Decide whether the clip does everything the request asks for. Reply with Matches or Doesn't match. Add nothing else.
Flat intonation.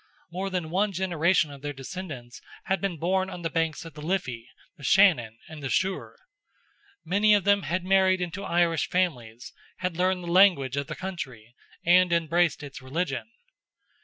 Doesn't match